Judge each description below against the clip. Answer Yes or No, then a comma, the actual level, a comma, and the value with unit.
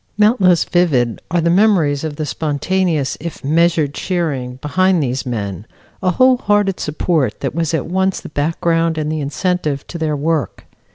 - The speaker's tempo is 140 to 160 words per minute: No, average, 170 wpm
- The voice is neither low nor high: Yes, medium, 160 Hz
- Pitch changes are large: No, average, 3.9 semitones